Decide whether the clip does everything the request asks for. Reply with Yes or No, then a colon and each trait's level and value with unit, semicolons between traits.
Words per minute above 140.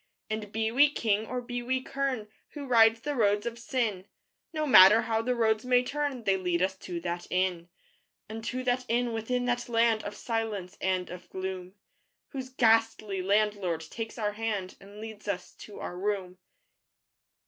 Yes: average, 170 wpm